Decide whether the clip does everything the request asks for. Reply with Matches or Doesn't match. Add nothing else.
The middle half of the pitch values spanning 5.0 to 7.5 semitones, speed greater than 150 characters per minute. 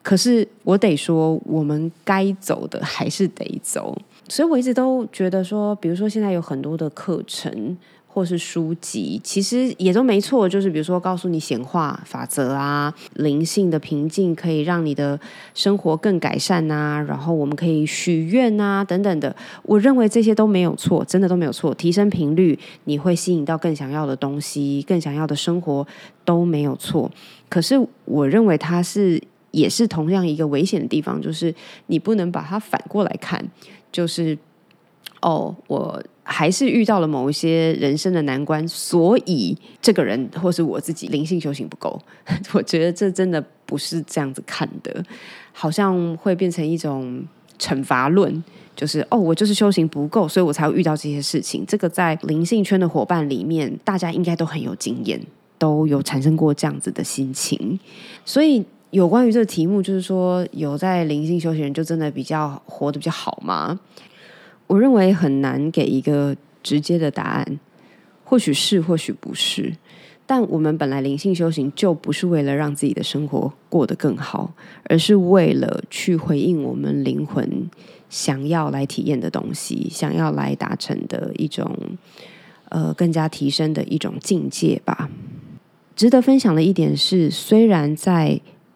Doesn't match